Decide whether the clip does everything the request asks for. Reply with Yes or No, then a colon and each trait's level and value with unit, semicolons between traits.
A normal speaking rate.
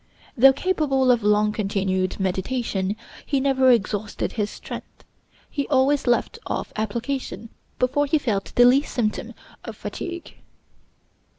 No: slow, 125 wpm